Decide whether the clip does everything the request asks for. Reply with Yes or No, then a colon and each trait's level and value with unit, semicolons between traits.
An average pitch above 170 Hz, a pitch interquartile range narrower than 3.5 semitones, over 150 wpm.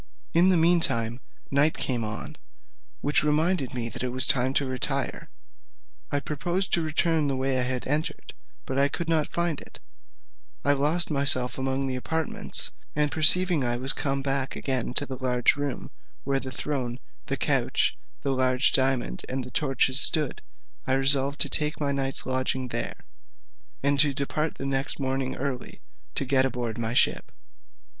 No: low, 135 Hz; narrow, 2.4 semitones; average, 170 wpm